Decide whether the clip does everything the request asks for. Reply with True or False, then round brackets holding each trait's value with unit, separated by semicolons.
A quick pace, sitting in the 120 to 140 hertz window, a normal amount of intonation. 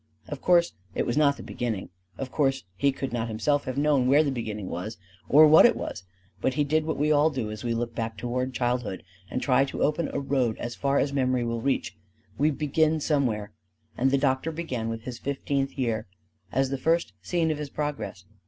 True (215 wpm; 135 Hz; 3.8 semitones)